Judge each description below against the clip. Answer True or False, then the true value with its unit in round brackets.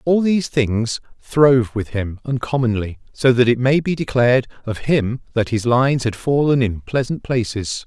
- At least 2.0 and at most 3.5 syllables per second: False (4.8 syllables/s)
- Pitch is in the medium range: False (125 Hz)